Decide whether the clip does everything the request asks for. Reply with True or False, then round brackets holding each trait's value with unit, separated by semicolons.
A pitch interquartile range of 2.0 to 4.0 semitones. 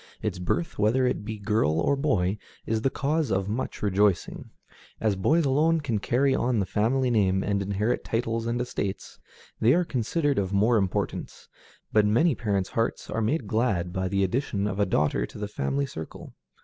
False (4.6 semitones)